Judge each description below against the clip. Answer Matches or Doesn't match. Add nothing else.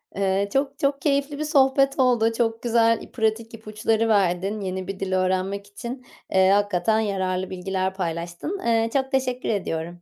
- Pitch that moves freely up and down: Doesn't match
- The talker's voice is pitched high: Matches